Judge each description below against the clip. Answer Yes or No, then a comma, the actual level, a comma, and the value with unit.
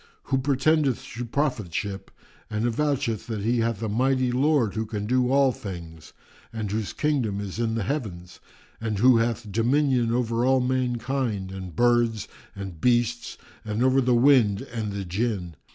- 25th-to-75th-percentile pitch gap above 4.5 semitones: No, average, 3.7 semitones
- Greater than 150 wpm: Yes, average, 165 wpm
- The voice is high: No, low, 115 Hz